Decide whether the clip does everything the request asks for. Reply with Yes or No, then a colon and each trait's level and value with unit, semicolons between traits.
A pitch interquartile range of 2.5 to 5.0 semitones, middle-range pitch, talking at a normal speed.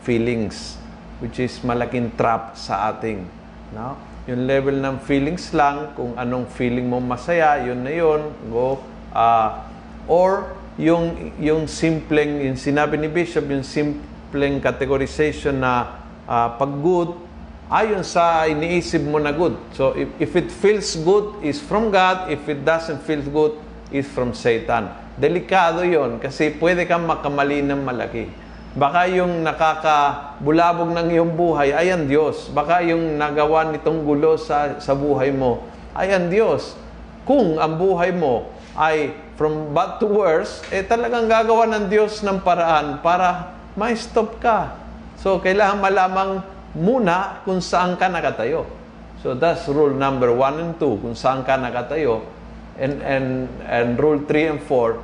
Yes: average, 4.6 semitones; medium, 155 Hz; average, 145 wpm